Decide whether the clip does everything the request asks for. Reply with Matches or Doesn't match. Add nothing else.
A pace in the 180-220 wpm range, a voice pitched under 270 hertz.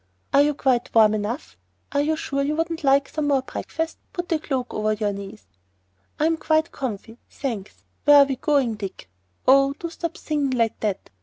Doesn't match